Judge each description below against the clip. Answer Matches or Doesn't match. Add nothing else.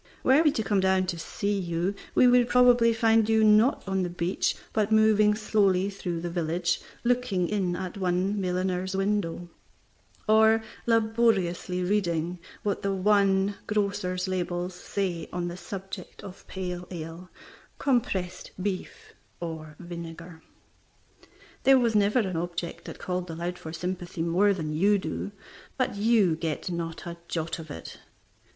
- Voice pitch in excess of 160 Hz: Matches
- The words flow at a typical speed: Matches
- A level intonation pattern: Doesn't match